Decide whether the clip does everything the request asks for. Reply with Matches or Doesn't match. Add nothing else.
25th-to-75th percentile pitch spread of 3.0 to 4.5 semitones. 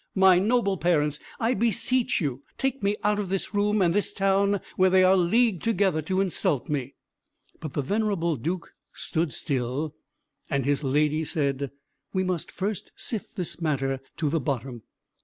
Doesn't match